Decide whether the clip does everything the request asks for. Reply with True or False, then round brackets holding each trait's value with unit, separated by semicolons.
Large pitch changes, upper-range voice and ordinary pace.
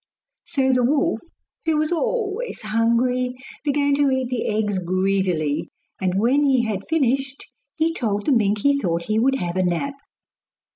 True (5.9 semitones; 250 Hz; 160 wpm)